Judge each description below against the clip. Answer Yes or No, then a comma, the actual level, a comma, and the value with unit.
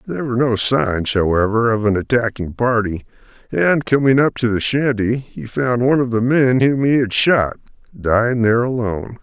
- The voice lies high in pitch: No, low, 120 Hz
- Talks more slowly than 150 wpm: No, average, 180 wpm